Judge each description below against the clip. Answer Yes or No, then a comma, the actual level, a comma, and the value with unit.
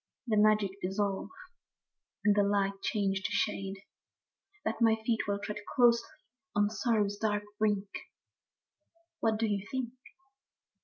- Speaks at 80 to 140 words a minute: Yes, slow, 135 wpm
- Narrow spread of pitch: Yes, narrow, 1.9 semitones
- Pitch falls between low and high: No, high, 210 Hz